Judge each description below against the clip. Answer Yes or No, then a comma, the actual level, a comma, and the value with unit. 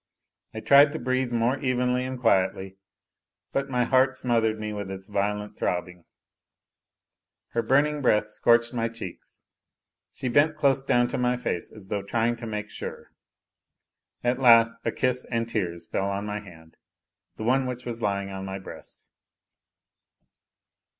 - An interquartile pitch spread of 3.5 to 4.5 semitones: Yes, average, 3.8 semitones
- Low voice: Yes, low, 115 Hz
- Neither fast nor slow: Yes, average, 155 wpm